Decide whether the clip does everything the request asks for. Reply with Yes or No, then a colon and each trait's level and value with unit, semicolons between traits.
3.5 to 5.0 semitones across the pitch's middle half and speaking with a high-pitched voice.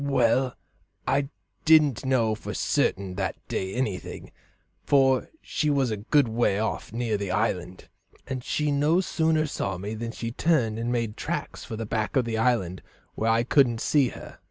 No: average, 4.1 semitones; low, 120 Hz